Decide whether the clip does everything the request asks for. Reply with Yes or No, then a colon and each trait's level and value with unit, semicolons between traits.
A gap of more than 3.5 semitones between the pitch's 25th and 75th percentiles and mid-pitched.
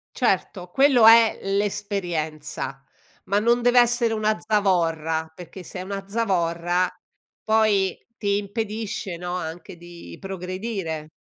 No: average, 3.9 semitones; high, 195 Hz